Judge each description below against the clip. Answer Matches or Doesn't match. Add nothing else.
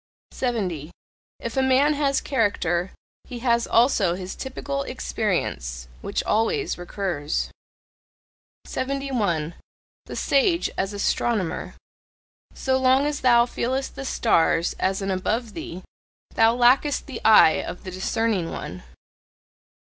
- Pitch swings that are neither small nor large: Doesn't match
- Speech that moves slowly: Matches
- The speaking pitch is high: Matches